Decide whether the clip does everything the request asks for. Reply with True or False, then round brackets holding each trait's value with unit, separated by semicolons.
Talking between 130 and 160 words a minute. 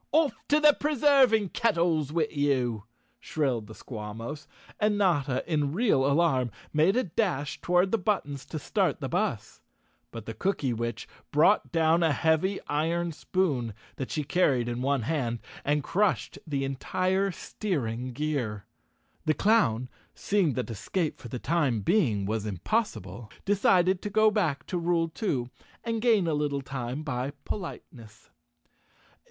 True (150 wpm)